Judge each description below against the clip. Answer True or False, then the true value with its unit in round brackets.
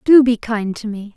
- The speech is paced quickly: True (260 wpm)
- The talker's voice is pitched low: False (225 Hz)